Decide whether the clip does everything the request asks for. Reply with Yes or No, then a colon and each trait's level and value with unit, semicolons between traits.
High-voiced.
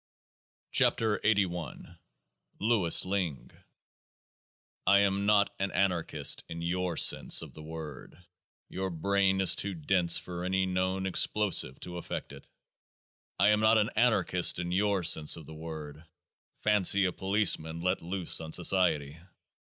No: very low, 90 Hz